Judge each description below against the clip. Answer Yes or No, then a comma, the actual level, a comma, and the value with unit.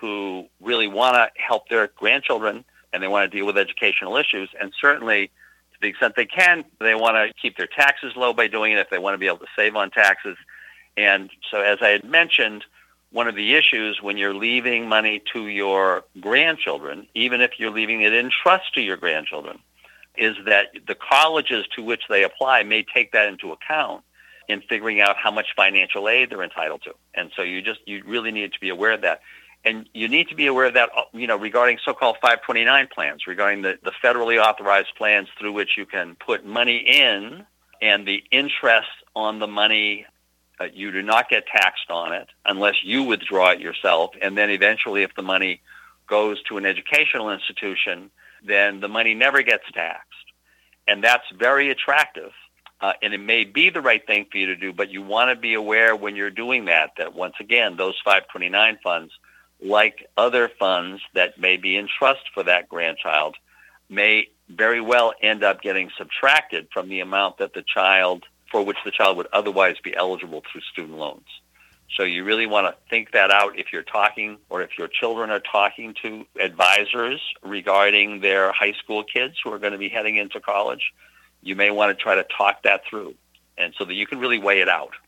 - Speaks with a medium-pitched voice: No, low, 105 Hz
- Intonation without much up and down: Yes, narrow, 2.3 semitones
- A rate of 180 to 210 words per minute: Yes, average, 200 wpm